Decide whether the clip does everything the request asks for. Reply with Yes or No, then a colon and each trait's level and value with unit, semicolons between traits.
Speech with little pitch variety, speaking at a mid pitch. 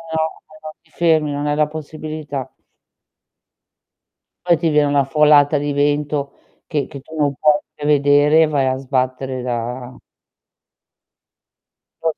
Yes: narrow, 1.8 semitones; medium, 145 Hz